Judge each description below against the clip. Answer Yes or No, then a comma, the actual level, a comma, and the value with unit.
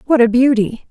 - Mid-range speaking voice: No, high, 245 Hz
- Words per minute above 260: No, average, 200 wpm